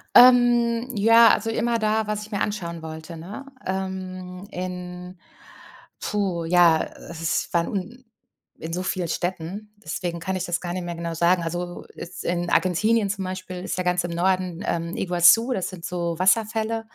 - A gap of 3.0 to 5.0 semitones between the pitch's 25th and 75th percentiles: Yes, average, 3.5 semitones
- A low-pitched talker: No, medium, 185 Hz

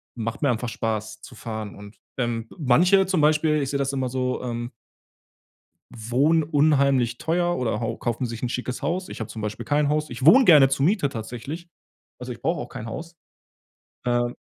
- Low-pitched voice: Yes, low, 130 Hz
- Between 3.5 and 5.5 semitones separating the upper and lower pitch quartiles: Yes, average, 4.5 semitones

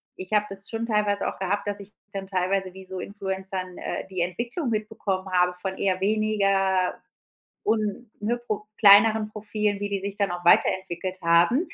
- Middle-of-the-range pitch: No, high, 195 Hz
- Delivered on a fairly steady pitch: Yes, narrow, 2.0 semitones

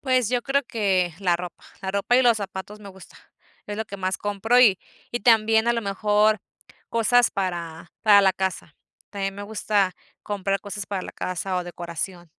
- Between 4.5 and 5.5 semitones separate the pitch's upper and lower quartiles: No, average, 2.8 semitones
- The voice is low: No, high, 200 Hz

